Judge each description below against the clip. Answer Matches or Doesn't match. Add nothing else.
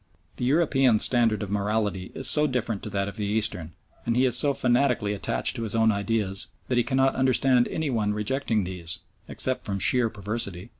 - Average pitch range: Matches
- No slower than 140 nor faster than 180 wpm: Doesn't match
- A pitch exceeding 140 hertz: Doesn't match